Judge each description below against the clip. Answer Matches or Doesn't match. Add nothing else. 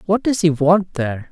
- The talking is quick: Matches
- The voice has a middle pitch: Matches